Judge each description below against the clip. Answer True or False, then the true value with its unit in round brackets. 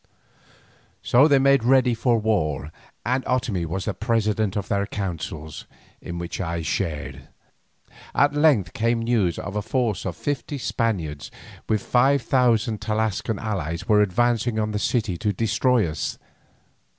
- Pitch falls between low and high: False (110 Hz)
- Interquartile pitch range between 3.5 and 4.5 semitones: False (4.9 semitones)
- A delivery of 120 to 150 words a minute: True (145 wpm)